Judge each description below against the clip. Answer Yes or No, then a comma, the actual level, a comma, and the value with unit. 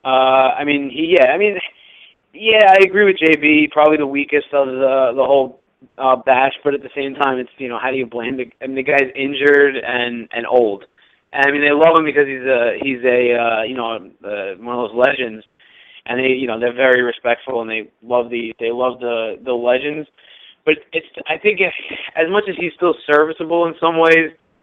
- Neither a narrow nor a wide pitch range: Yes, average, 3.8 semitones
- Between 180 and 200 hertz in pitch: No, low, 135 Hz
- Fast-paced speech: Yes, fast, 220 wpm